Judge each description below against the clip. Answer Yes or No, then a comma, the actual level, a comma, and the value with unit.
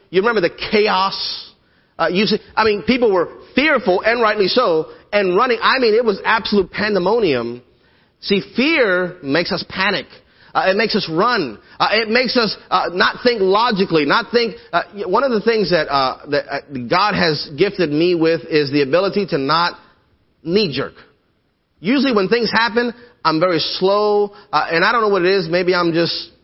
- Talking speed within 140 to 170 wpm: No, average, 185 wpm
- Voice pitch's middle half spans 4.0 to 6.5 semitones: Yes, average, 5.1 semitones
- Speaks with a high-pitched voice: Yes, high, 195 Hz